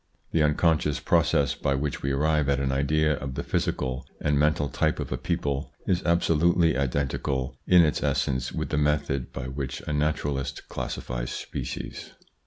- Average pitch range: No, narrow, 2.1 semitones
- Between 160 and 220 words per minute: Yes, average, 170 wpm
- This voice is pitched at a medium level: No, very low, 70 Hz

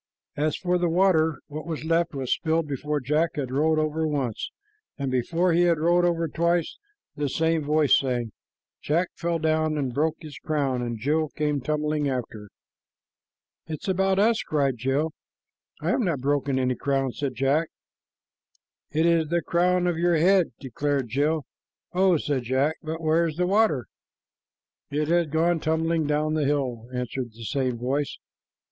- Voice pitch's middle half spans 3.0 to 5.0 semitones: Yes, average, 3.3 semitones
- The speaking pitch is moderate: Yes, medium, 155 Hz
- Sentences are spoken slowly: No, average, 165 wpm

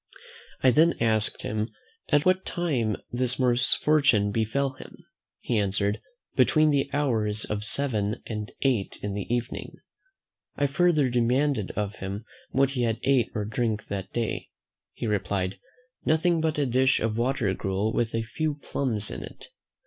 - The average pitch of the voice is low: Yes, low, 120 Hz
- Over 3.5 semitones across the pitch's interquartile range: Yes, average, 4.7 semitones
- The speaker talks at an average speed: Yes, average, 155 wpm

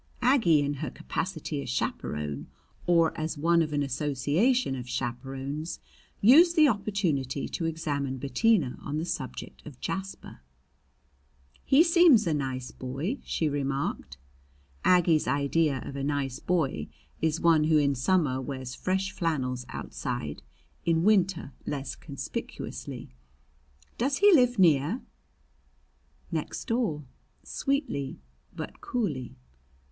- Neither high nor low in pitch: Yes, medium, 150 Hz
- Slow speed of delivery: Yes, slow, 120 wpm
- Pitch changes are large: Yes, wide, 5.9 semitones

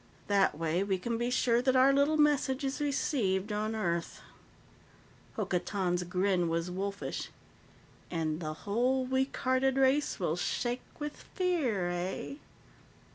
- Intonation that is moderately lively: No, wide, 6.7 semitones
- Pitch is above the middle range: Yes, high, 215 Hz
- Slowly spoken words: Yes, slow, 130 wpm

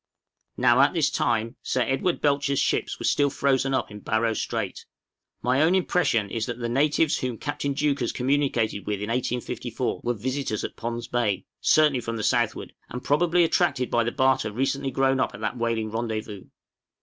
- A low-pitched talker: Yes, low, 125 Hz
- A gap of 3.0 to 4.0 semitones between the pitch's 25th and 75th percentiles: Yes, average, 3.6 semitones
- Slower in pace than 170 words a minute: No, average, 180 wpm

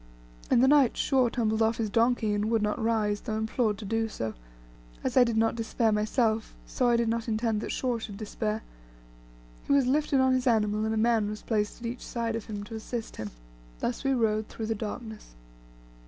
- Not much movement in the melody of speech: Yes, narrow, 1.8 semitones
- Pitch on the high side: Yes, high, 225 Hz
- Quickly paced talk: Yes, fast, 215 wpm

